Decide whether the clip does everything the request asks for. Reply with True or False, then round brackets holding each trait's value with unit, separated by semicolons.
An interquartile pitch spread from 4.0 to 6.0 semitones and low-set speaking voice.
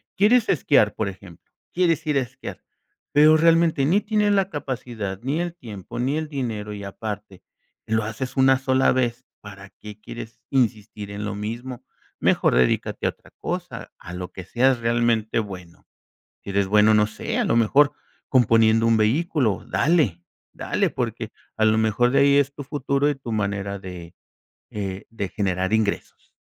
True (5.2 semitones; 115 Hz)